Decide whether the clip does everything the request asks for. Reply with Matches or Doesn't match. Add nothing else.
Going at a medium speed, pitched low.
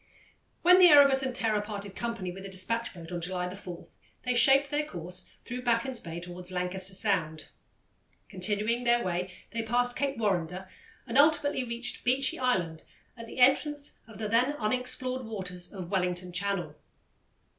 Doesn't match